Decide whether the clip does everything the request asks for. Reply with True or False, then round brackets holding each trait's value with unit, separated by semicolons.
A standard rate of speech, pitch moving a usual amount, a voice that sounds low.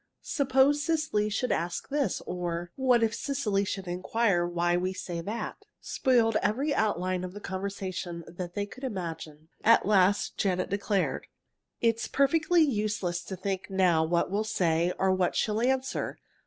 False (155 wpm; 4.7 semitones; 200 Hz)